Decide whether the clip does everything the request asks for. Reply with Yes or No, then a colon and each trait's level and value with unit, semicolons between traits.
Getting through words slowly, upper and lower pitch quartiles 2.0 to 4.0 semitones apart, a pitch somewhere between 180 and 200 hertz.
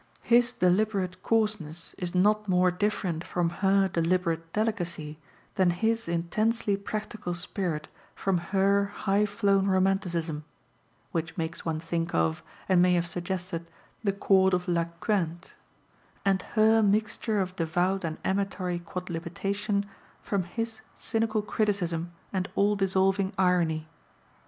Yes: slow, 125 wpm; average, 3.0 semitones; high, 190 Hz